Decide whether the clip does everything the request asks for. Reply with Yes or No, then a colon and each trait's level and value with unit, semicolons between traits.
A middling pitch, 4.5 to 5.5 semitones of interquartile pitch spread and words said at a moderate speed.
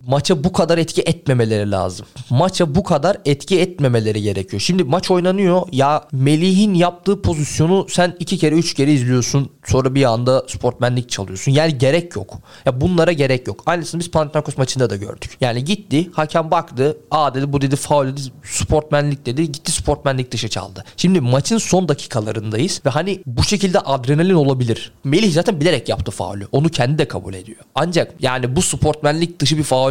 No: medium, 145 Hz; average, 5.2 semitones; fast, 175 wpm